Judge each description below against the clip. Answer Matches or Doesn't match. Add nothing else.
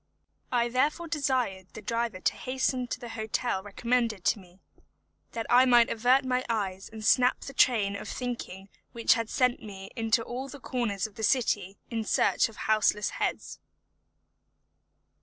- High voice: Matches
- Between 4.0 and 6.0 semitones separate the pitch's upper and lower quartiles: Doesn't match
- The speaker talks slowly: Doesn't match